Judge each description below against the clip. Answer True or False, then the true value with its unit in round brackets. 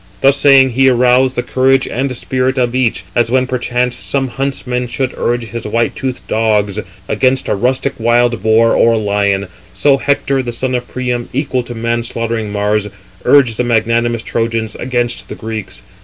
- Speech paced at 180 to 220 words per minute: False (170 wpm)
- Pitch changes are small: True (2.2 semitones)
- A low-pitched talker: True (120 Hz)